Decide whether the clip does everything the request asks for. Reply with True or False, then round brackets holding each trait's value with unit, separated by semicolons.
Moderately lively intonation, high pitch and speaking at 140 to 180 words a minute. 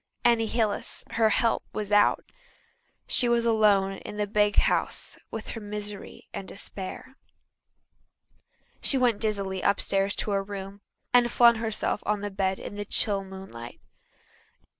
False (2.3 semitones; 205 Hz; 145 wpm)